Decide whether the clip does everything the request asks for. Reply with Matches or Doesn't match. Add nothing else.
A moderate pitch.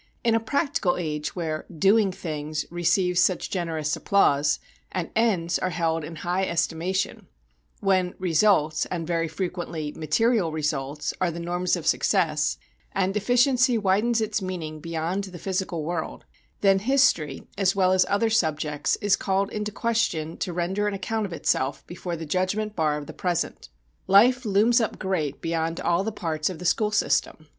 Matches